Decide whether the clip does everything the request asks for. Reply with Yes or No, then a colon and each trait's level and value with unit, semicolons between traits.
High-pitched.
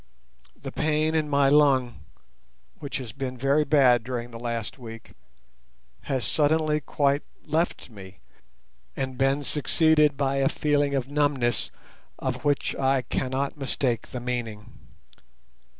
No: low, 135 Hz